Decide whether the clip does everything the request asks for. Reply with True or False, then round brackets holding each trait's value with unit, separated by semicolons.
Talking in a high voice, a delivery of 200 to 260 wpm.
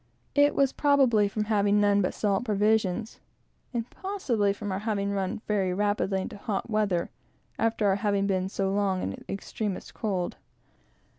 False (205 Hz; 155 wpm)